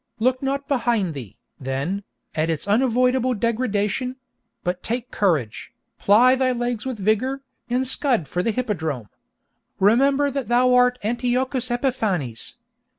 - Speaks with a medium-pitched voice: No, high, 240 Hz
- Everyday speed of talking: No, slow, 130 wpm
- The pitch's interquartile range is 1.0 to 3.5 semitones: No, average, 4.4 semitones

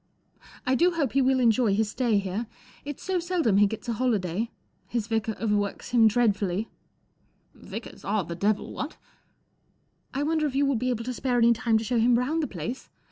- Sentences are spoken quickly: Yes, fast, 215 wpm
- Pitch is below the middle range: No, high, 235 Hz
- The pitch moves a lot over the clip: No, average, 3.7 semitones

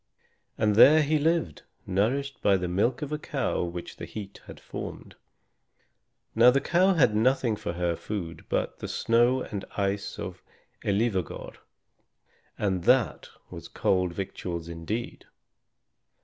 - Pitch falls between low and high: No, low, 105 Hz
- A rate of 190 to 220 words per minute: No, slow, 135 wpm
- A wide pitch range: Yes, wide, 6.0 semitones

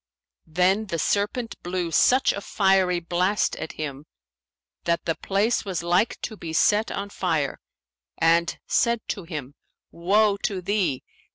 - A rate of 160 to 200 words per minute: No, average, 145 wpm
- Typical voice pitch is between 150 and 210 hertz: Yes, medium, 185 Hz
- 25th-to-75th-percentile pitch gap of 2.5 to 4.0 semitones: Yes, average, 3.4 semitones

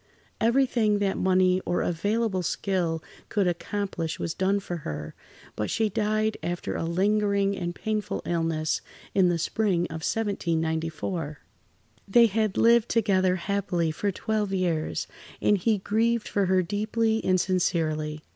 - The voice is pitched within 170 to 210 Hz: Yes, high, 190 Hz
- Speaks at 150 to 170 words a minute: No, slow, 135 wpm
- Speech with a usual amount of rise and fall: Yes, average, 3.9 semitones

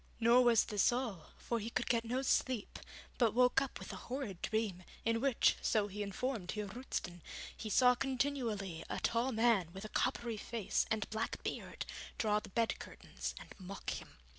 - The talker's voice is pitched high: Yes, high, 230 Hz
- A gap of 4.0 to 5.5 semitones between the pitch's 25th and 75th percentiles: No, average, 3.3 semitones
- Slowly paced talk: No, average, 185 wpm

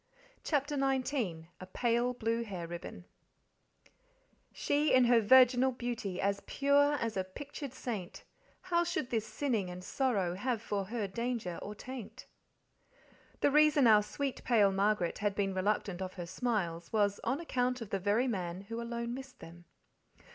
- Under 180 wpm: Yes, average, 155 wpm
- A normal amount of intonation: Yes, average, 4.8 semitones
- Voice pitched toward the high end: Yes, high, 230 Hz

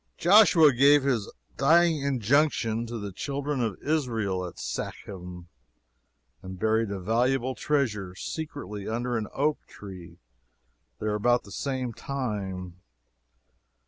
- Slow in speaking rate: Yes, slow, 115 wpm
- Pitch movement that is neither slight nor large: No, wide, 5.7 semitones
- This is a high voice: No, low, 115 Hz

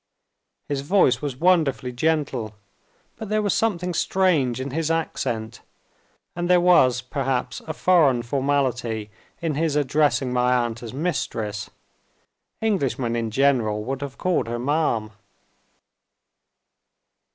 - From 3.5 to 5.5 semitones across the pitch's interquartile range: Yes, average, 5.2 semitones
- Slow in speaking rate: Yes, slow, 120 wpm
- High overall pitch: No, low, 135 Hz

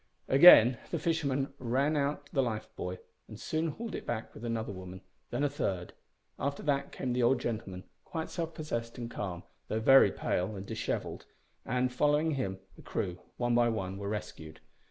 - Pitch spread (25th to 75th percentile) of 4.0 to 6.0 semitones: Yes, average, 5.3 semitones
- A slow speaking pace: No, average, 180 wpm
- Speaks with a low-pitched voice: Yes, low, 120 Hz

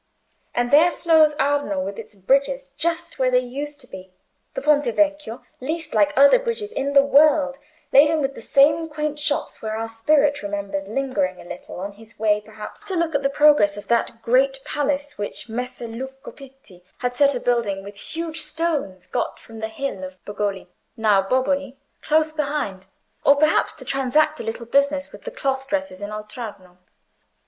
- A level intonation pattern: No, wide, 5.4 semitones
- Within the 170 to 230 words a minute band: Yes, average, 180 wpm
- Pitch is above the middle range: Yes, very high, 270 Hz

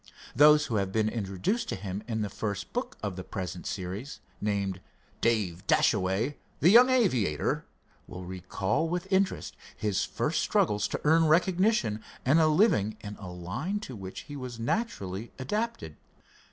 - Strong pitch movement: Yes, wide, 8.7 semitones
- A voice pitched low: Yes, low, 110 Hz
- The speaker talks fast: No, average, 155 wpm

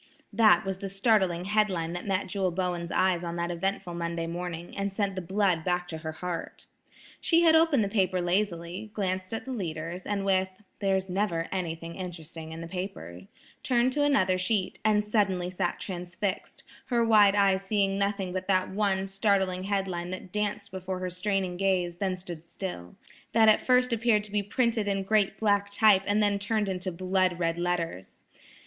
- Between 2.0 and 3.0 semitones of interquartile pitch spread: Yes, narrow, 2.6 semitones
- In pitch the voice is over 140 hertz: Yes, high, 190 Hz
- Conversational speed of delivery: Yes, average, 185 wpm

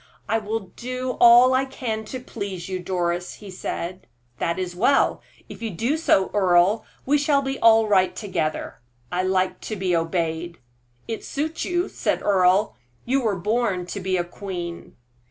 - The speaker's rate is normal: Yes, average, 170 wpm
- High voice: Yes, high, 200 Hz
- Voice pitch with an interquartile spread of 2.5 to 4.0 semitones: No, average, 4.8 semitones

